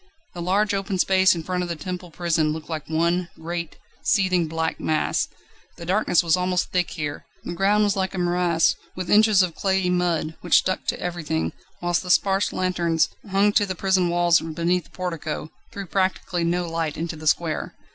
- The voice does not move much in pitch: Yes, narrow, 2.2 semitones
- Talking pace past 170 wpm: Yes, average, 190 wpm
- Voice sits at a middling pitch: Yes, medium, 175 Hz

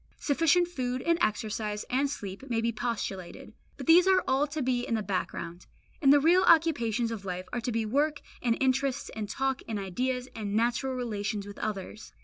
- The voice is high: Yes, high, 245 Hz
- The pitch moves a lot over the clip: No, average, 4.6 semitones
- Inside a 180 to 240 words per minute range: Yes, average, 190 wpm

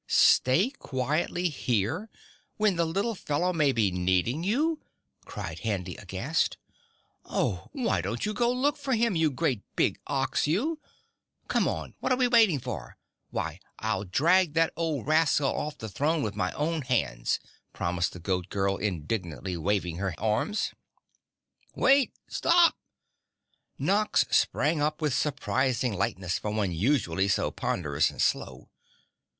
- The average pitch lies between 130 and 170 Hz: Yes, medium, 140 Hz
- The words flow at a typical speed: Yes, average, 145 wpm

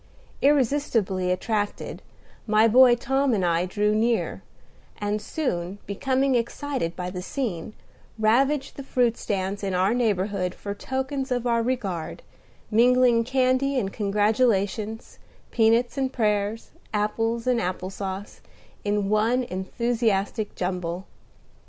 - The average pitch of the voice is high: Yes, high, 220 Hz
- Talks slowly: Yes, slow, 115 wpm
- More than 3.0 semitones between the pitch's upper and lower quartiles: Yes, average, 4.2 semitones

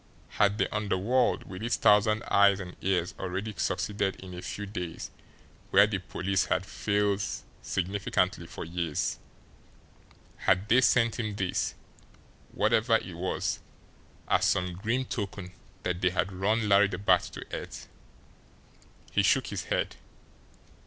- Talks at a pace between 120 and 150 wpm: Yes, average, 140 wpm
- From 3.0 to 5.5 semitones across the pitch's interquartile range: No, narrow, 2.5 semitones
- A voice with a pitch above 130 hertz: No, low, 100 Hz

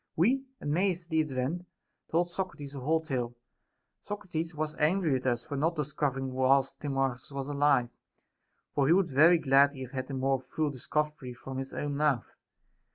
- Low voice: No, medium, 145 Hz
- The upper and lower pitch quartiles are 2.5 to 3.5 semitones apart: Yes, average, 3.2 semitones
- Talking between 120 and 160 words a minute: No, average, 185 wpm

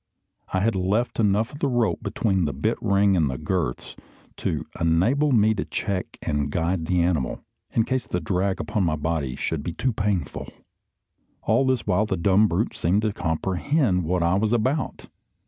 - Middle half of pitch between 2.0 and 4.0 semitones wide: No, average, 4.7 semitones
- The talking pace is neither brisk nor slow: Yes, average, 180 wpm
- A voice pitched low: Yes, very low, 95 Hz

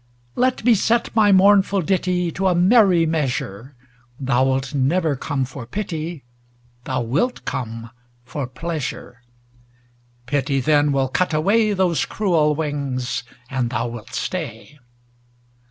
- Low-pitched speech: No, medium, 150 Hz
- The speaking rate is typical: No, slow, 125 wpm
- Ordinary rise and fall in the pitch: No, wide, 6.1 semitones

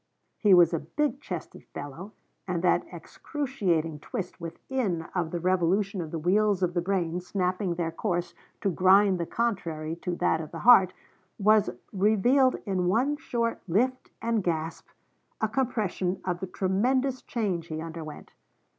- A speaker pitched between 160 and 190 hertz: Yes, medium, 185 Hz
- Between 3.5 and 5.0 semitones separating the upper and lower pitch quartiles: Yes, average, 4.2 semitones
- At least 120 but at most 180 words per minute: Yes, average, 155 wpm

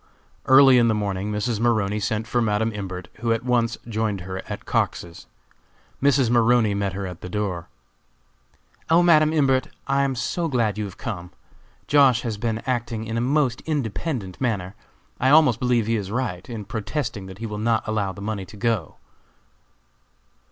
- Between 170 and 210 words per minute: Yes, average, 175 wpm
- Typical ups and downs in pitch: Yes, average, 3.5 semitones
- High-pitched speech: No, low, 115 Hz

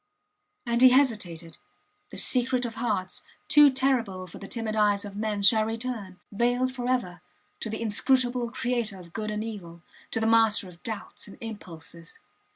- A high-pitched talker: Yes, high, 220 Hz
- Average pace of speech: Yes, average, 160 wpm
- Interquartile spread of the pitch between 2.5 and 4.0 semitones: Yes, average, 3.7 semitones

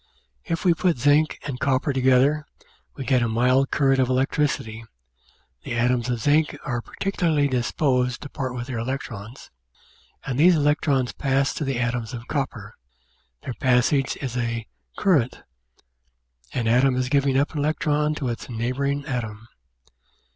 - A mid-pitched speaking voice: No, low, 130 Hz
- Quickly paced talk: No, average, 155 wpm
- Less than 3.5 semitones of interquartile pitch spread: Yes, average, 2.8 semitones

